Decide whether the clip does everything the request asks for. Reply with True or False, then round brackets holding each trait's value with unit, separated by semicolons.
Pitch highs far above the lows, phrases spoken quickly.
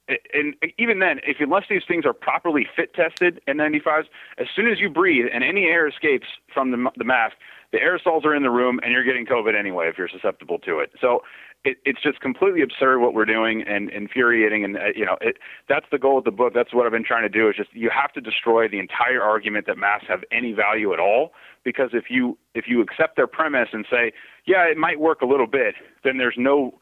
True (7.3 semitones; 235 wpm)